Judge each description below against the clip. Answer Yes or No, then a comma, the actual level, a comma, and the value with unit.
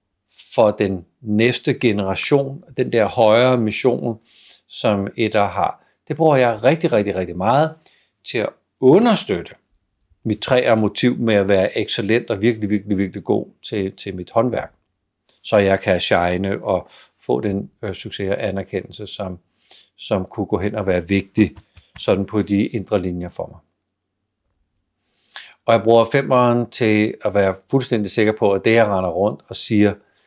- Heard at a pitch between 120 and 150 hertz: No, low, 105 Hz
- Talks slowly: No, average, 155 wpm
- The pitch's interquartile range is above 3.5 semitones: No, average, 2.9 semitones